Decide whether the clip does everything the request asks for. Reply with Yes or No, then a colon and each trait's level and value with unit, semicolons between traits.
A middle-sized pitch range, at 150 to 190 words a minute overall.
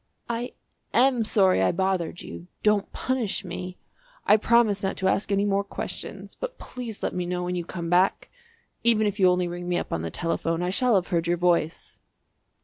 No: average, 3.3 semitones; average, 200 wpm